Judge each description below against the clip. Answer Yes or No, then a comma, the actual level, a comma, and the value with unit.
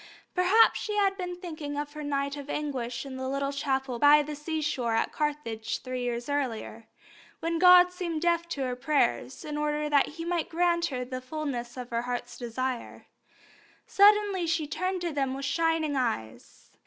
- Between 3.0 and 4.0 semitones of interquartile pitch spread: No, average, 4.7 semitones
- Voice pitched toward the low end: No, very high, 290 Hz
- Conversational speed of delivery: Yes, average, 180 wpm